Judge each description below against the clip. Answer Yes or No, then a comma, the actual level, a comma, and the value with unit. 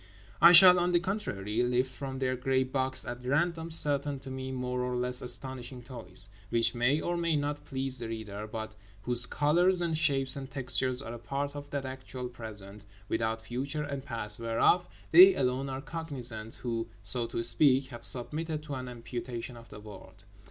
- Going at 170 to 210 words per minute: Yes, average, 175 wpm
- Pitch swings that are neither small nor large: Yes, average, 3.5 semitones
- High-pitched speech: No, low, 130 Hz